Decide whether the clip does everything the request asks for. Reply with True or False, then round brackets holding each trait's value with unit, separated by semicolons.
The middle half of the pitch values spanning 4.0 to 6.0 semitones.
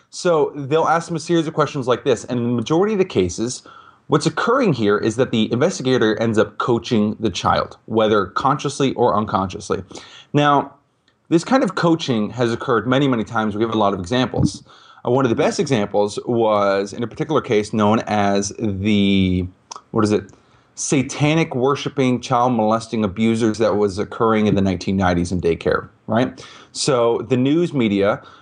True (4.7 semitones)